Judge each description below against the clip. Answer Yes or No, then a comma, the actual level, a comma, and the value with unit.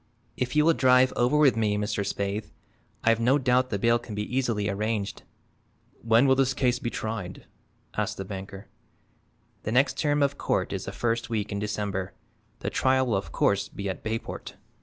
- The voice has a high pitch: No, low, 115 Hz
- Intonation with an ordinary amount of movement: Yes, average, 3.9 semitones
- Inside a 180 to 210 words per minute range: Yes, average, 185 wpm